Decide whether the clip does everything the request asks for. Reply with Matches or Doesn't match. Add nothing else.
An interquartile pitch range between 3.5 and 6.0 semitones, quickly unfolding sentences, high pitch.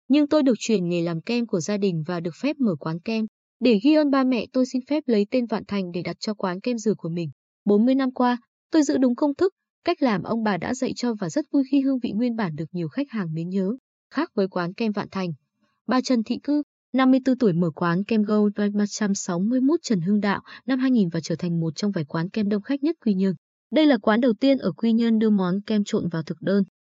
Matches